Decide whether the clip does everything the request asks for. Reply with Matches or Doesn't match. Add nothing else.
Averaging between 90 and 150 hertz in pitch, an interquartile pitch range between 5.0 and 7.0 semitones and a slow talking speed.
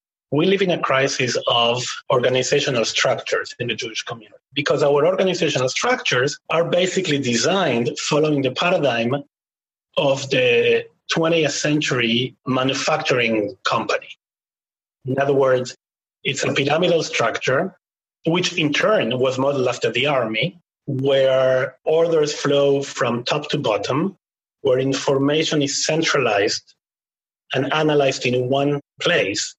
Doesn't match